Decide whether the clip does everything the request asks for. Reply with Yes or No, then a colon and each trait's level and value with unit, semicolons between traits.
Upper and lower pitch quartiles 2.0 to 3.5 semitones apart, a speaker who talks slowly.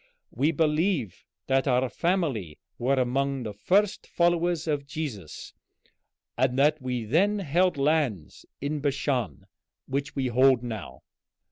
No: average, 4.3 semitones; slow, 125 wpm